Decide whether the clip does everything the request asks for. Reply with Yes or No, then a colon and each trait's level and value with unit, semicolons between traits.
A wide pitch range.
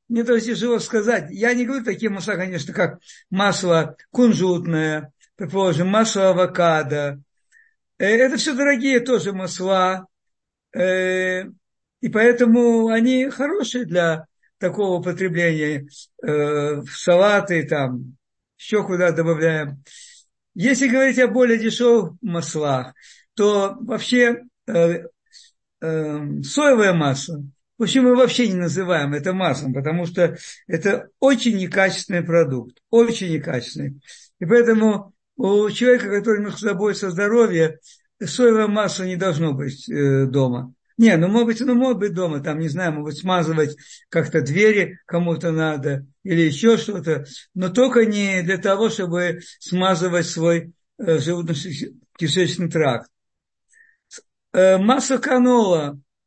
Yes: wide, 5.9 semitones